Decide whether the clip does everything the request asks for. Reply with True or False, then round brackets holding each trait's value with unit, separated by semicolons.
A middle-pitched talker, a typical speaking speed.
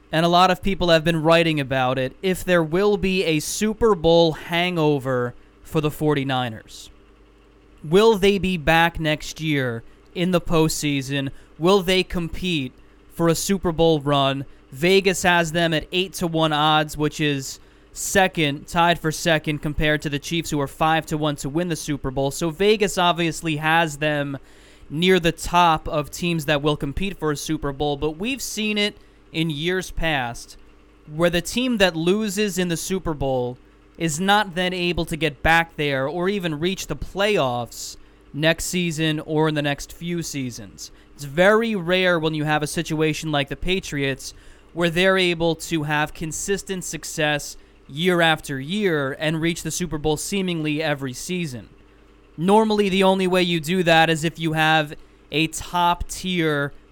True (160 Hz; 170 wpm)